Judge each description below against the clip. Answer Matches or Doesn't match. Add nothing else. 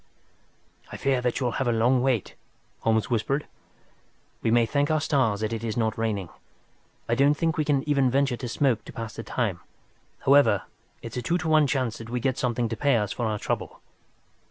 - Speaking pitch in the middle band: Doesn't match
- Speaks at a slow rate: Doesn't match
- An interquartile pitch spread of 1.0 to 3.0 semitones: Doesn't match